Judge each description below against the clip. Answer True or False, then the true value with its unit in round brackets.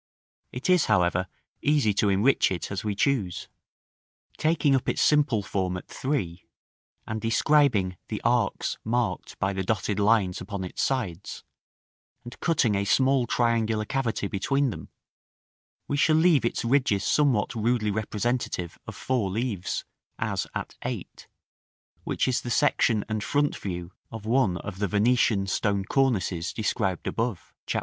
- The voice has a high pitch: False (110 Hz)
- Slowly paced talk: False (145 wpm)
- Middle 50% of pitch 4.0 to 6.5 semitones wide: True (4.9 semitones)